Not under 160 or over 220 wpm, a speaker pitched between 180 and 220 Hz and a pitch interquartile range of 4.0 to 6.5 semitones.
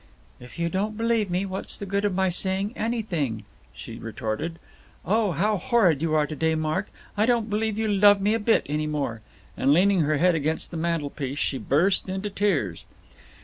Yes: average, 190 wpm; medium, 185 Hz; average, 5.1 semitones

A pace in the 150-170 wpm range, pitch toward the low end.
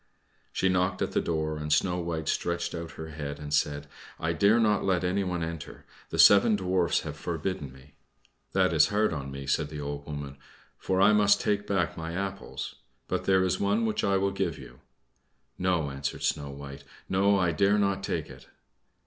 No: average, 190 wpm; very low, 85 Hz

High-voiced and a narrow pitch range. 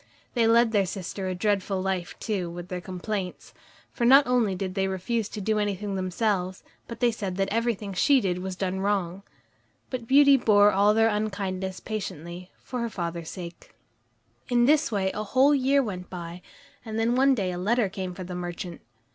No: high, 200 Hz; average, 3.7 semitones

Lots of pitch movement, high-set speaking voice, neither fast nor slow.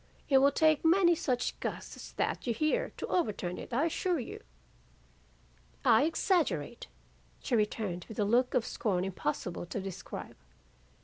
Yes: wide, 7.9 semitones; high, 240 Hz; average, 160 wpm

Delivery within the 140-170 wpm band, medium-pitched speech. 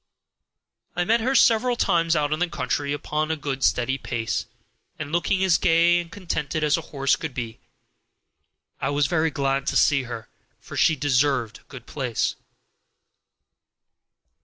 Yes: average, 160 wpm; medium, 150 Hz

